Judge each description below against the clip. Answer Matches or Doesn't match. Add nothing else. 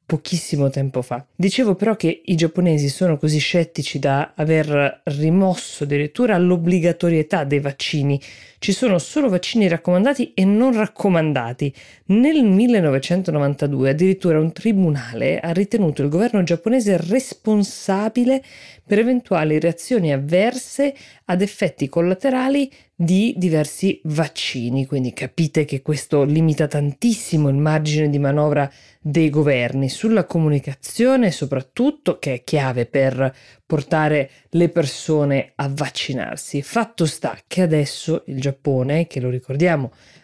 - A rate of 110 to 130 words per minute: Matches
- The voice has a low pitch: Doesn't match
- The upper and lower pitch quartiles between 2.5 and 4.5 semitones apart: Doesn't match